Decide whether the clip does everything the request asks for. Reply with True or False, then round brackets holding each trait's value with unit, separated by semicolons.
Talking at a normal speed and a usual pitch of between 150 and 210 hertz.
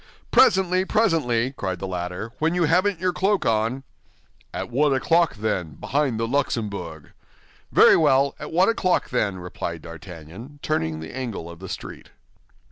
False (150 wpm; 125 Hz)